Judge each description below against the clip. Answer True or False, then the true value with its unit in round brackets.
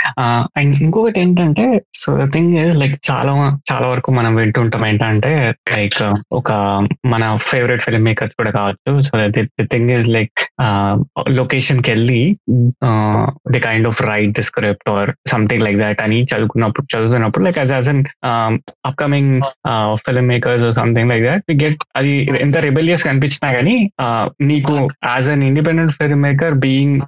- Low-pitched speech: True (125 Hz)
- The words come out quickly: True (135 wpm)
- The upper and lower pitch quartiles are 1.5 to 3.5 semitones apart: False (4.0 semitones)